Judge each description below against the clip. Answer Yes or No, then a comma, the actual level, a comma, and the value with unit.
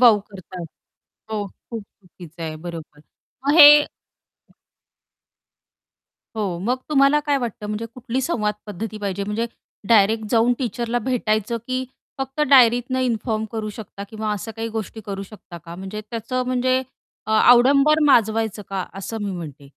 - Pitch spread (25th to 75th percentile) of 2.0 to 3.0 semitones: No, average, 3.7 semitones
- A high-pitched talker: Yes, high, 220 Hz